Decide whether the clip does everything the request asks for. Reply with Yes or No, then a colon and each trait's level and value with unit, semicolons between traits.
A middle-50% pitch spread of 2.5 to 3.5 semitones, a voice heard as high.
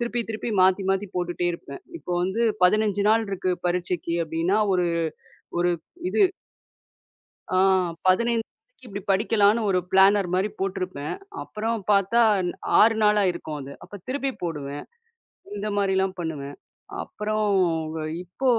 Yes: average, 3.2 semitones; high, 195 Hz